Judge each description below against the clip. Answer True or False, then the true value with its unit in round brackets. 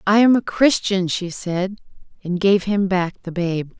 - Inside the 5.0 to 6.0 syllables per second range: False (4.2 syllables/s)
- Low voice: False (190 Hz)